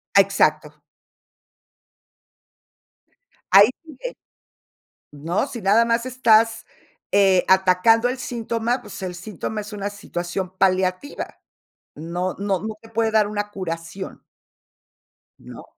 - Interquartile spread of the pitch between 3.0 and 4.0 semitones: Yes, average, 3.6 semitones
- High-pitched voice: Yes, high, 200 Hz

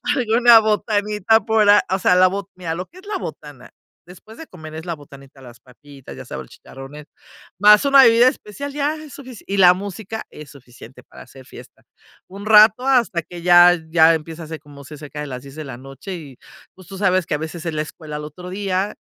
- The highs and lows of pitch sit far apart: Yes, wide, 6.0 semitones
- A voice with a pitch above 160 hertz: Yes, medium, 180 Hz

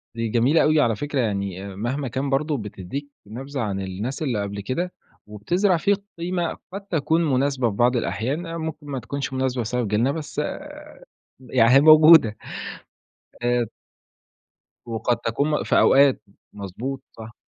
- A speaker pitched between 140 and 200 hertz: No, low, 130 Hz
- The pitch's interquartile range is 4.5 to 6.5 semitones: Yes, average, 5.1 semitones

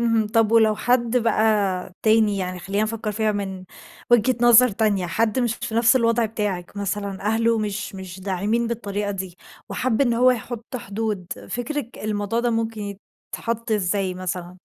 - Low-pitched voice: No, high, 215 Hz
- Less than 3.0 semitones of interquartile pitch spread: Yes, narrow, 2.5 semitones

